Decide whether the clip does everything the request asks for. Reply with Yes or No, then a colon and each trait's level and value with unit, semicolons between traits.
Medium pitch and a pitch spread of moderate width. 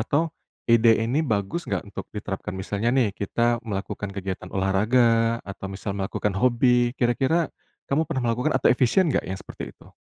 No: low, 115 Hz; average, 4.2 semitones